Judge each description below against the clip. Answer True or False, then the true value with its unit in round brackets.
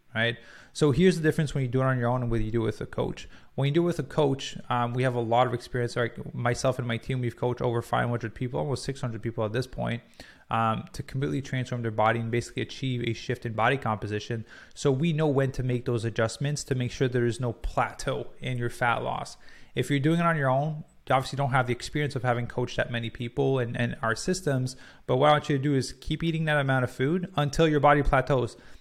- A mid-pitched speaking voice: False (130 Hz)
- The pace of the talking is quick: True (260 wpm)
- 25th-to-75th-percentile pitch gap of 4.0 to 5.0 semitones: False (3.0 semitones)